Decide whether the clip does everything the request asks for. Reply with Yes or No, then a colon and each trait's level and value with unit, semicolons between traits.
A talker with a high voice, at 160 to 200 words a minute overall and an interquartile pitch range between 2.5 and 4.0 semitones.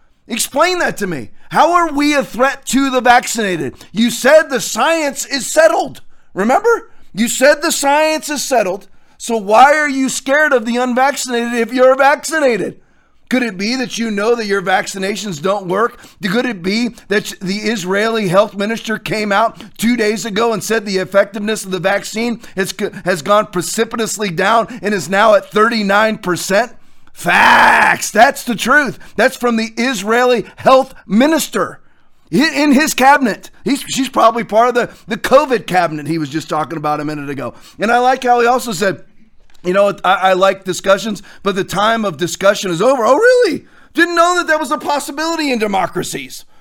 No: high, 230 Hz; average, 180 wpm; average, 5.1 semitones